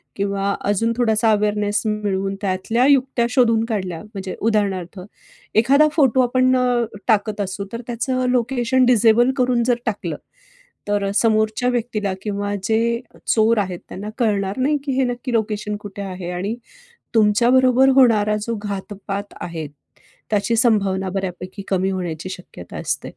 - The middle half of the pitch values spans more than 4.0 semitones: No, average, 3.5 semitones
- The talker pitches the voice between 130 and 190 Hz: No, high, 215 Hz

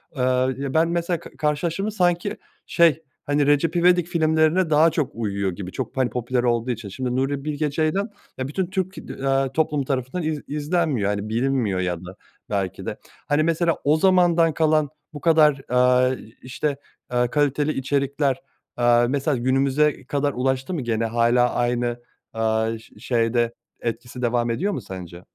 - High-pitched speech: No, low, 135 Hz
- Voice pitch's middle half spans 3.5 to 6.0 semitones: Yes, average, 4.6 semitones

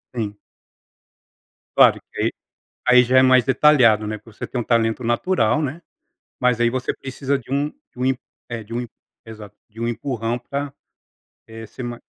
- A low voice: Yes, low, 120 Hz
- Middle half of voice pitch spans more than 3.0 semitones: No, narrow, 2.6 semitones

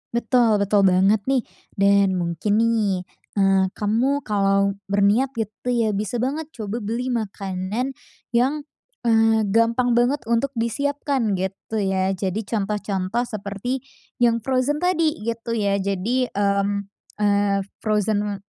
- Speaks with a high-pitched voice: Yes, high, 215 Hz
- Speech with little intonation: No, average, 3.4 semitones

